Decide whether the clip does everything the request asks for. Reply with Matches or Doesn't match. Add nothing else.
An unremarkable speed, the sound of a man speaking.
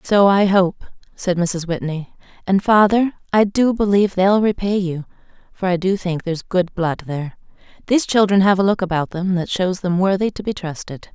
Doesn't match